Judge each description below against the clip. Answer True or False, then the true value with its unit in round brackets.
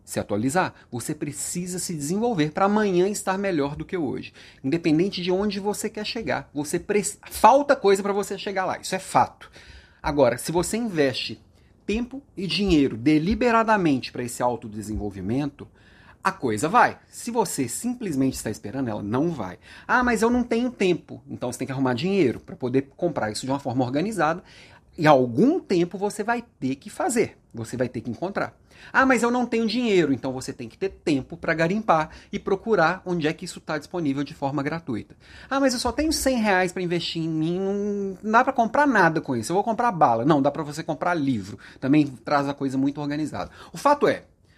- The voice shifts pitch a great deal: True (7.3 semitones)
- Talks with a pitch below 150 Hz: False (170 Hz)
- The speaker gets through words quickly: True (200 wpm)